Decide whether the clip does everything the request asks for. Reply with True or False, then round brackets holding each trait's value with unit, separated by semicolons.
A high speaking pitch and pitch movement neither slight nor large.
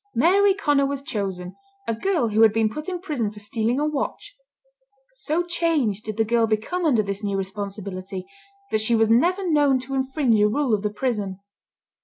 False (230 Hz; 6.1 semitones)